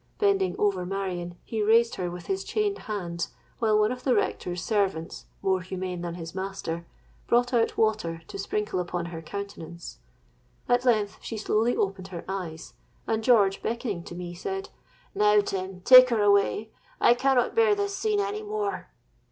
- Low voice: No, high, 205 Hz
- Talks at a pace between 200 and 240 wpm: No, average, 170 wpm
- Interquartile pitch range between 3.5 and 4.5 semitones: No, average, 5.2 semitones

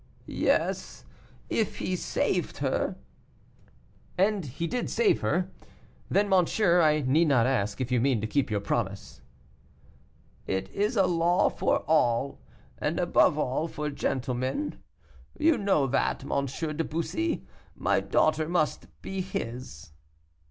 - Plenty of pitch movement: Yes, wide, 6.3 semitones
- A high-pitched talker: No, medium, 155 Hz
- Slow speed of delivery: Yes, slow, 130 wpm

